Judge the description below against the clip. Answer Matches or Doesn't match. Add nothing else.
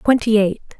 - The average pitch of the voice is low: Doesn't match